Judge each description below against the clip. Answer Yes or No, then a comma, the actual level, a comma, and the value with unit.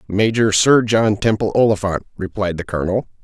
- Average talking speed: Yes, average, 150 wpm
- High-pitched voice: No, low, 105 Hz